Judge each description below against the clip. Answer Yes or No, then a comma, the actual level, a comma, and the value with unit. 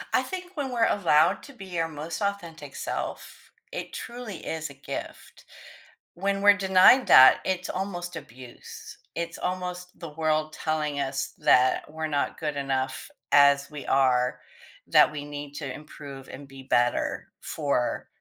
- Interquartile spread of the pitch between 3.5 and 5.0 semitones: Yes, average, 4.7 semitones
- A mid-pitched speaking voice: Yes, medium, 155 Hz